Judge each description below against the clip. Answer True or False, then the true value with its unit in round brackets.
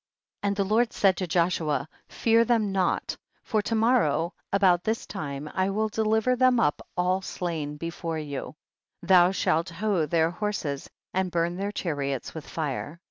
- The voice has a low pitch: False (180 Hz)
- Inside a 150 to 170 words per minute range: True (165 wpm)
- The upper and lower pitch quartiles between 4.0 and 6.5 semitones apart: True (4.6 semitones)